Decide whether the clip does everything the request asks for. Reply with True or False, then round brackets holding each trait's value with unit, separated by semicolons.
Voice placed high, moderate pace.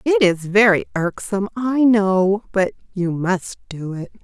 True (200 Hz; 155 wpm)